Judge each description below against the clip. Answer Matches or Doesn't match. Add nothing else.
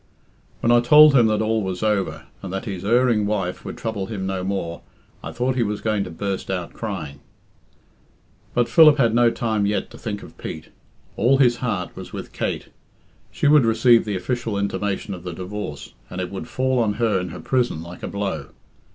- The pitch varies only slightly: Doesn't match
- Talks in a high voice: Doesn't match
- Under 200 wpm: Doesn't match